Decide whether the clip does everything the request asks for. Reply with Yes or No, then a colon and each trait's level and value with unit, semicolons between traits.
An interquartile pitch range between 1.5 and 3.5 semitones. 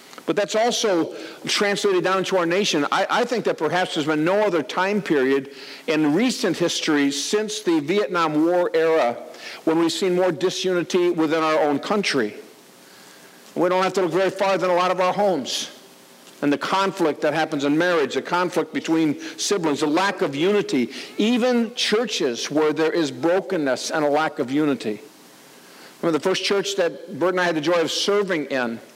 No: average, 4.4 semitones